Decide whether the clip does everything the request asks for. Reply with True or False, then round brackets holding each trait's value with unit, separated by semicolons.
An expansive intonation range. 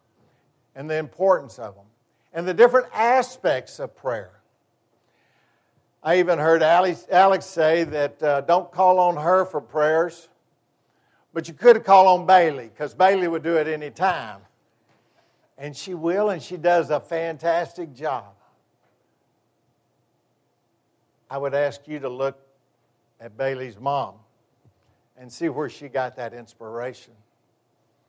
True (6.5 semitones)